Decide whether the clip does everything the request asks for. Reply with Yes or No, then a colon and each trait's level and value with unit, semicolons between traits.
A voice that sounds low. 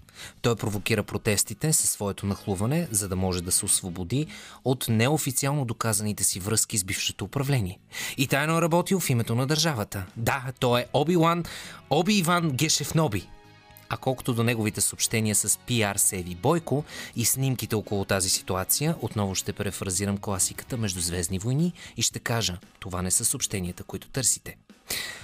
Yes: low, 110 Hz